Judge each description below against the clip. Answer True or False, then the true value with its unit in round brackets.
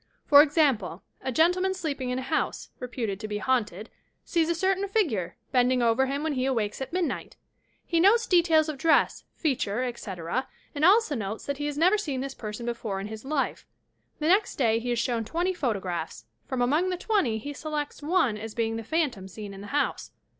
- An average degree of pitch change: False (6.3 semitones)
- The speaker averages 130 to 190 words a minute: False (205 wpm)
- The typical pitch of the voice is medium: False (265 Hz)